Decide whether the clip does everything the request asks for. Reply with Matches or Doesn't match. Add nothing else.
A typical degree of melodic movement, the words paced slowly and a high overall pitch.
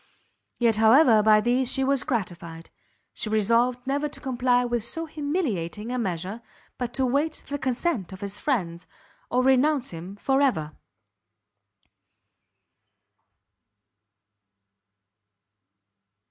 Matches